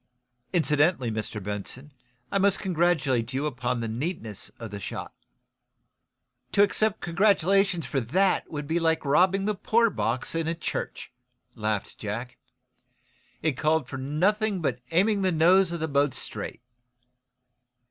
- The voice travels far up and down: Yes, wide, 6.8 semitones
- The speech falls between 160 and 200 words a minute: No, average, 140 wpm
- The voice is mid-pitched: Yes, medium, 160 Hz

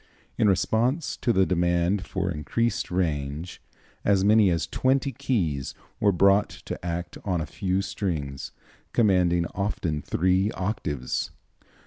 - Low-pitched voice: Yes, very low, 95 Hz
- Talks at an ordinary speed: No, slow, 125 wpm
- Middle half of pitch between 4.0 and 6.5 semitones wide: No, average, 3.3 semitones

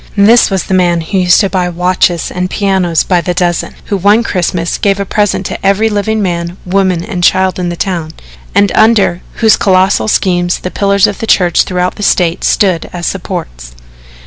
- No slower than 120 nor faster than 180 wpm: No, average, 195 wpm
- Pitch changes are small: Yes, narrow, 2.2 semitones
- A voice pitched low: No, medium, 185 Hz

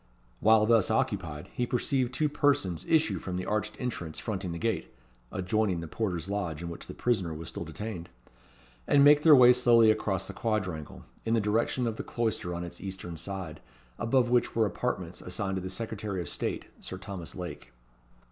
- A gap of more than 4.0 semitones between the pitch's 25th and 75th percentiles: Yes, average, 5.0 semitones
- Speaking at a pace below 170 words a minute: No, average, 185 wpm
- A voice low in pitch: Yes, low, 105 Hz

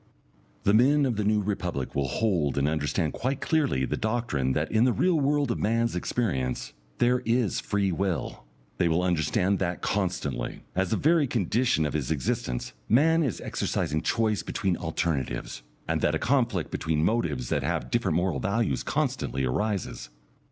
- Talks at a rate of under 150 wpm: No, average, 165 wpm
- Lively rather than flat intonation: Yes, wide, 7.2 semitones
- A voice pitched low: Yes, very low, 95 Hz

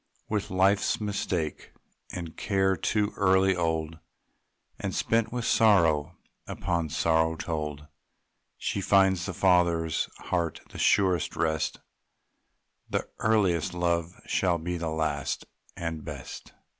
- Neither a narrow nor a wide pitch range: Yes, average, 3.0 semitones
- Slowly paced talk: Yes, slow, 115 wpm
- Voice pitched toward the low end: Yes, very low, 85 Hz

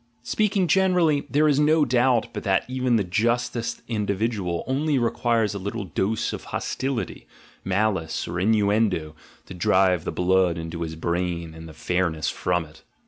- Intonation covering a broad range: Yes, wide, 5.9 semitones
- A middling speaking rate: Yes, average, 160 wpm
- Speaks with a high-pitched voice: No, low, 100 Hz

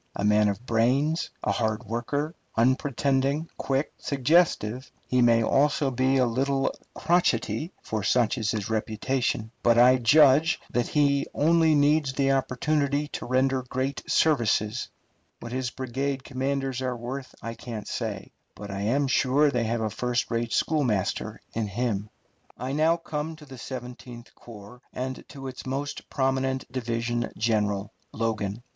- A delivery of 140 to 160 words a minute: Yes, average, 150 wpm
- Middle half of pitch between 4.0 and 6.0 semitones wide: No, average, 3.3 semitones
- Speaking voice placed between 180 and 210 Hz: No, low, 130 Hz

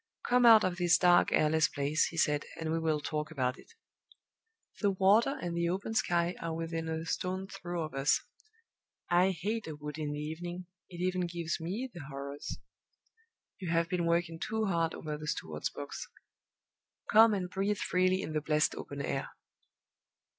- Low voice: No, medium, 170 Hz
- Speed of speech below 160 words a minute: No, average, 175 wpm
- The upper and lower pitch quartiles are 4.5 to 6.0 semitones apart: No, average, 3.0 semitones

